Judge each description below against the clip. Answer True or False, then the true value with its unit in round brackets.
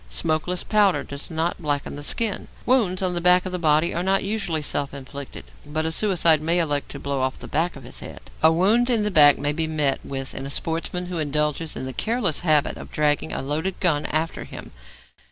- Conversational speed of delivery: False (225 wpm)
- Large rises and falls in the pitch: False (3.6 semitones)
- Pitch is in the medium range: True (160 Hz)